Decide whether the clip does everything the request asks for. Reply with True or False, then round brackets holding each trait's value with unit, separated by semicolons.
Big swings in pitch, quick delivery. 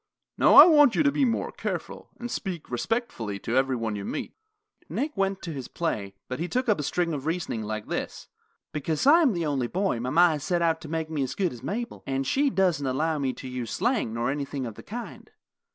True (7.2 semitones; 230 wpm)